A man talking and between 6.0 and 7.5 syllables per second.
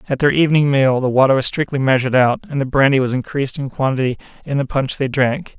Yes: male; 6.6 syllables/s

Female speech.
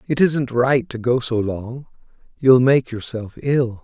No: male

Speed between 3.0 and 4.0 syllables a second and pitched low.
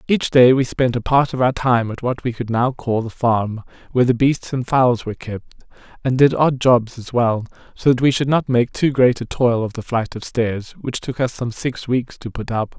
No: 4.9 syllables/s; low, 125 Hz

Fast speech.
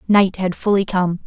No: average, 190 wpm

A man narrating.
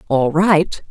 No: female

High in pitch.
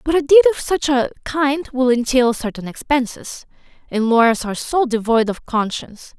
Yes: very high, 255 Hz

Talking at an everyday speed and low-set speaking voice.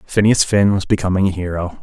Yes: average, 195 wpm; very low, 95 Hz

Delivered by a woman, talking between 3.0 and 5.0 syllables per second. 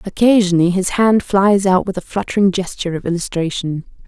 No: female; 5.8 syllables/s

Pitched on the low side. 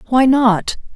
No: high, 235 Hz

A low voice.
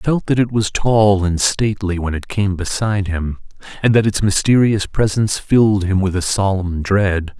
Yes: low, 100 Hz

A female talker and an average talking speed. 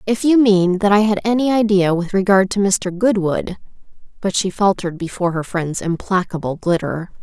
Yes: female; average, 175 wpm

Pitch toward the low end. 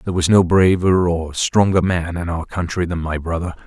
Yes: very low, 85 Hz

